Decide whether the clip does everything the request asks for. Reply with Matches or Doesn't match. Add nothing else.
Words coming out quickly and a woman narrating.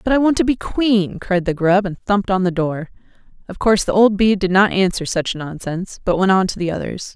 Matches